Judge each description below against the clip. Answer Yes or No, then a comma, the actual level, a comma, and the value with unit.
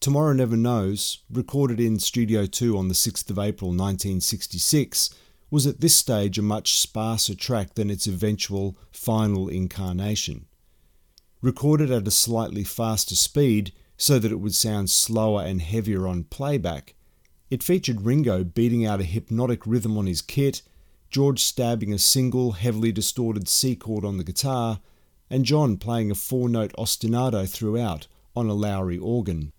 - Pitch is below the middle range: Yes, low, 110 Hz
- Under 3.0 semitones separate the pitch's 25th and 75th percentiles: No, average, 4.4 semitones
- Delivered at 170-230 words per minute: No, average, 150 wpm